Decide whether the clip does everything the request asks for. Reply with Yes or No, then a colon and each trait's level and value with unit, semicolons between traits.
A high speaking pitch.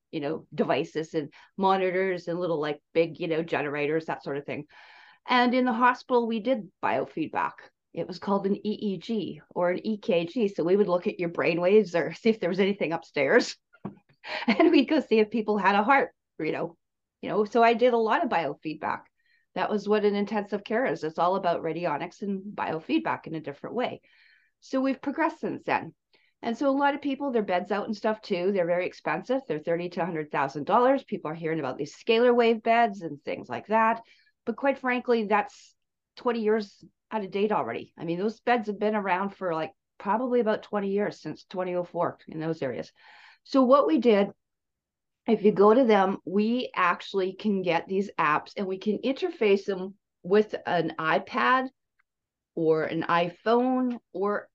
Yes: high, 205 Hz